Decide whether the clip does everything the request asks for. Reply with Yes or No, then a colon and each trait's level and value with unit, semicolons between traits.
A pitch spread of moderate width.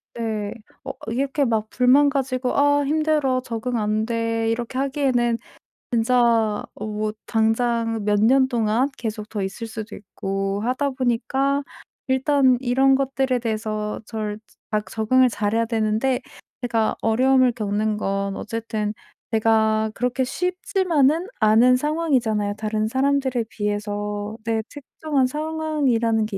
Yes: average, 3.5 semitones